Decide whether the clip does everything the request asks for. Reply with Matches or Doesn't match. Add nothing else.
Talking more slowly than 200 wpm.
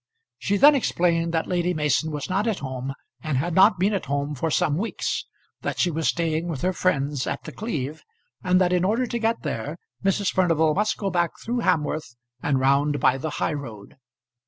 Doesn't match